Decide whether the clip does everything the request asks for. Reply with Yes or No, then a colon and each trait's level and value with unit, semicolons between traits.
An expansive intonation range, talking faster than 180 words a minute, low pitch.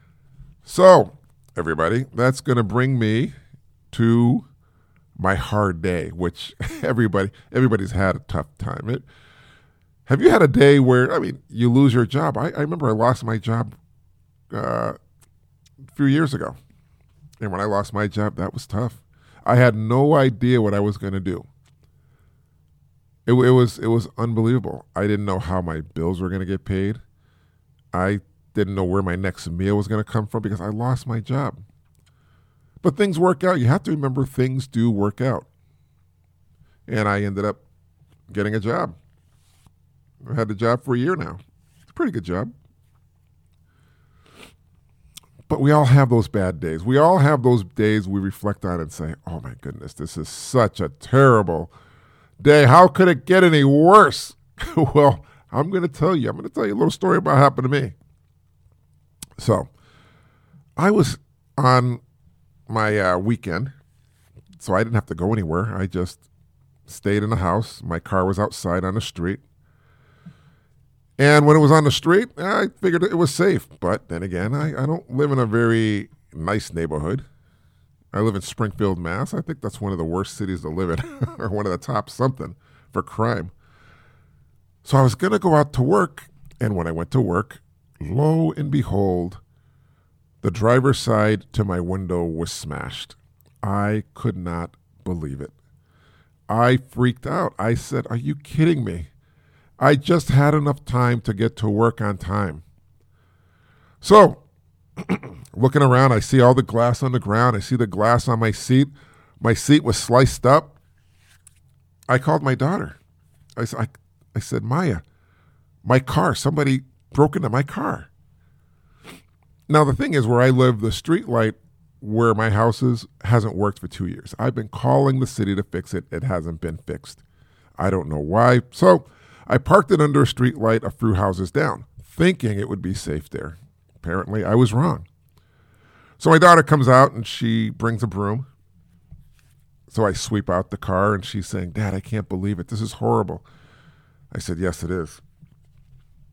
No: wide, 5.8 semitones; average, 175 wpm; low, 110 Hz